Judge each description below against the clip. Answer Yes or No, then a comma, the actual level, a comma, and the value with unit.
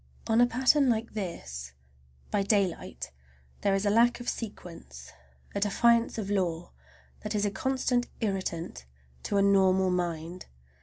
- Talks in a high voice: Yes, high, 200 Hz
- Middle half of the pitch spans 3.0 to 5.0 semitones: Yes, average, 4.5 semitones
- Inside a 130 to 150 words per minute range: Yes, average, 145 wpm